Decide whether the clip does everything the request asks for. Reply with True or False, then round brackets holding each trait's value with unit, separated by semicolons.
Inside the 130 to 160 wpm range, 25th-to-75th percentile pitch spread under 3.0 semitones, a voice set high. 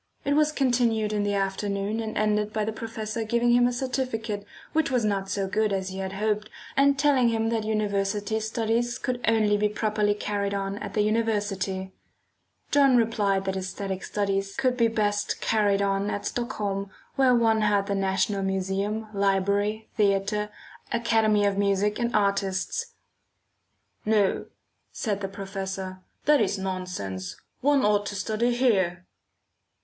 True (155 wpm; 2.4 semitones; 210 Hz)